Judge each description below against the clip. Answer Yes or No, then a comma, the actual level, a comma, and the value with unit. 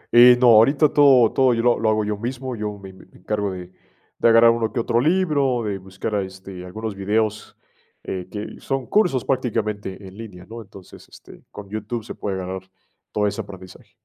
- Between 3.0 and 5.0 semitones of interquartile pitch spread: Yes, average, 3.7 semitones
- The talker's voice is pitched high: No, low, 110 Hz